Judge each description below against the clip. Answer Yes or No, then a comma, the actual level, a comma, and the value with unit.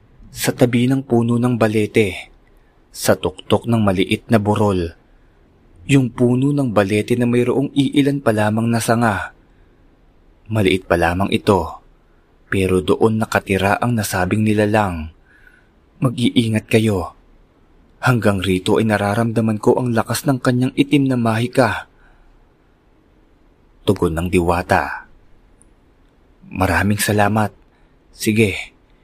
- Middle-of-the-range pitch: No, low, 110 Hz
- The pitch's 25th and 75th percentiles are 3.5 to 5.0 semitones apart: Yes, average, 4.2 semitones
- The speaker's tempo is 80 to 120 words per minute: Yes, slow, 110 wpm